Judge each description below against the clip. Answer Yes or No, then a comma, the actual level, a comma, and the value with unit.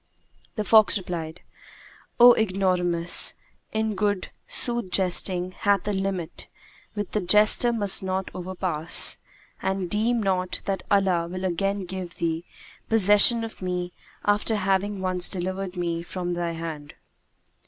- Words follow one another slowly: Yes, slow, 130 wpm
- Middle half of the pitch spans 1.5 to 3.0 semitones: Yes, narrow, 2.6 semitones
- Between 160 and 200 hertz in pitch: Yes, high, 190 Hz